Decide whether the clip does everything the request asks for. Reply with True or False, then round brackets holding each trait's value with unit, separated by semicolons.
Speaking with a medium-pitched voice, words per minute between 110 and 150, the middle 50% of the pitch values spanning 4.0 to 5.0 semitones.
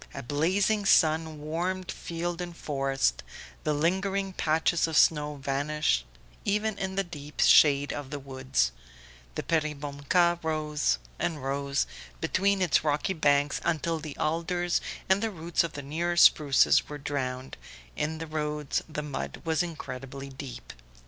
False (155 Hz; 140 wpm; 3.4 semitones)